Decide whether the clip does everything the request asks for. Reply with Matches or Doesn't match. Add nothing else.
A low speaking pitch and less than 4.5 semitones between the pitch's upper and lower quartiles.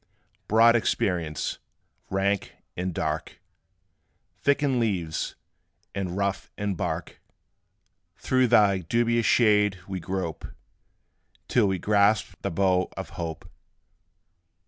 Matches